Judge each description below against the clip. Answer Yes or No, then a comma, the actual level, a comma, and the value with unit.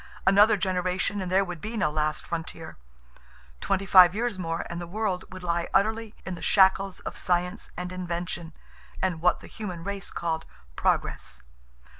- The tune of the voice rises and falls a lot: No, narrow, 2.4 semitones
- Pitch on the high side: No, medium, 180 Hz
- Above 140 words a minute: Yes, average, 165 wpm